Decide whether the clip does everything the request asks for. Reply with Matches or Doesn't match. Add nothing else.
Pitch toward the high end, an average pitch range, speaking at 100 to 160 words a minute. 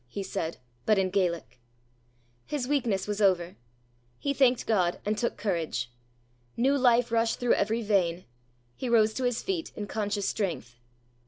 Matches